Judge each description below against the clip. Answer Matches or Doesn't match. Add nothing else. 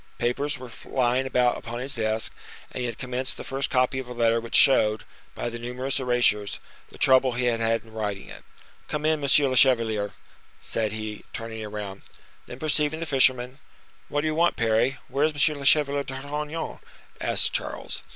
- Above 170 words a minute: Matches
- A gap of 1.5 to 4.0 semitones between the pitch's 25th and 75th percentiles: Matches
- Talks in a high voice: Doesn't match